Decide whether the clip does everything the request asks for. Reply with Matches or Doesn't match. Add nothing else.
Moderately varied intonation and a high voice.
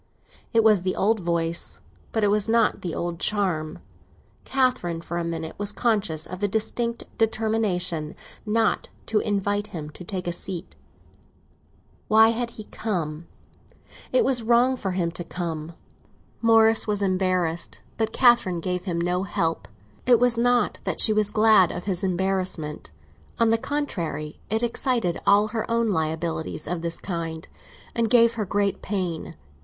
Matches